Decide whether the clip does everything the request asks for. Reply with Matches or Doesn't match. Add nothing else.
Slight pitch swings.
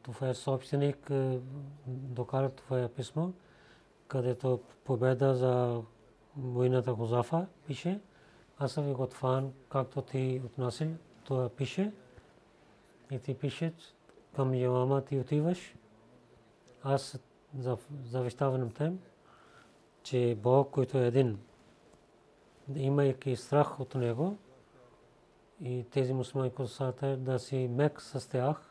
Matches